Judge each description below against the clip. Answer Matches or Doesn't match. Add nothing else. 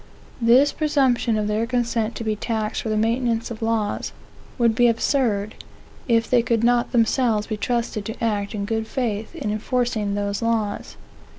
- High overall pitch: Matches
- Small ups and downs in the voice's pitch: Matches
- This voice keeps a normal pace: Matches